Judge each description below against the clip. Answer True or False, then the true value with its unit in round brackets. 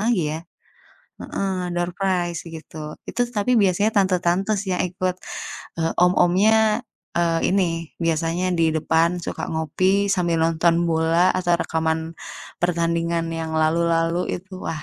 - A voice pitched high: False (175 Hz)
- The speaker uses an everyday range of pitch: False (2.2 semitones)